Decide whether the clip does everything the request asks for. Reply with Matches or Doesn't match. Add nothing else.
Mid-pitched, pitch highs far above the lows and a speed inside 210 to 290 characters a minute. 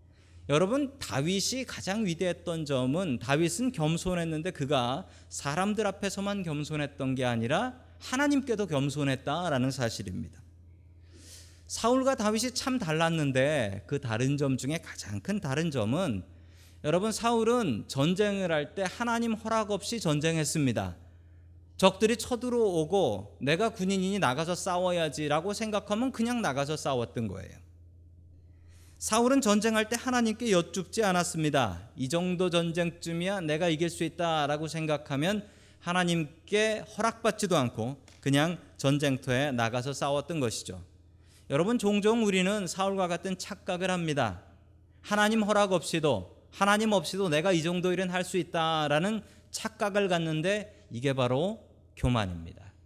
Doesn't match